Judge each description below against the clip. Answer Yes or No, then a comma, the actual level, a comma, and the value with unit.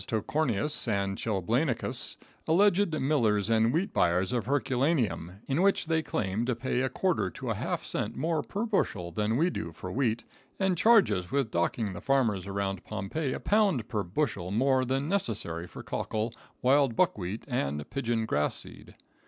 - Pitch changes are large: Yes, wide, 7.2 semitones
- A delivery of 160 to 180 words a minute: Yes, average, 170 wpm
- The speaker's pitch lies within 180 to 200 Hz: No, low, 120 Hz